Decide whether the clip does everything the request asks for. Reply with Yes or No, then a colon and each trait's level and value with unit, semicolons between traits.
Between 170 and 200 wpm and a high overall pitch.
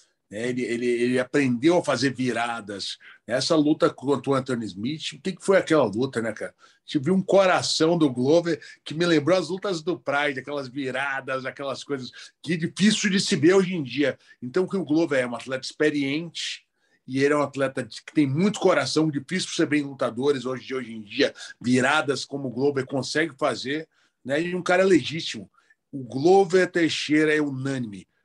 No: fast, 185 wpm; medium, 145 Hz